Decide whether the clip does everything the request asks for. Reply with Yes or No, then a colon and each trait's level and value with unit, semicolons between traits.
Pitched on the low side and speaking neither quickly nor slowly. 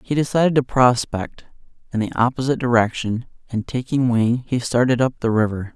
Yes: low, 125 Hz; average, 165 wpm